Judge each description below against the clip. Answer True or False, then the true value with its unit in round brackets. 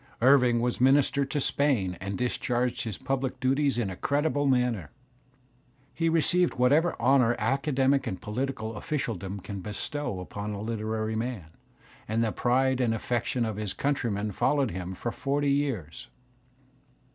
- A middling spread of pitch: True (4.3 semitones)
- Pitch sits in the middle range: False (125 Hz)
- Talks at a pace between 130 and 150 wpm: True (145 wpm)